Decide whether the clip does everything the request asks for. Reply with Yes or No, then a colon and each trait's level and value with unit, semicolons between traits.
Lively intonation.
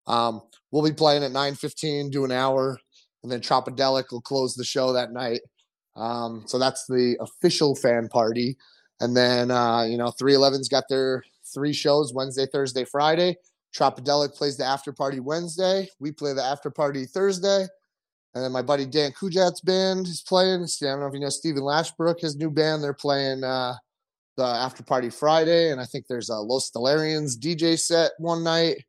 No: average, 3.4 semitones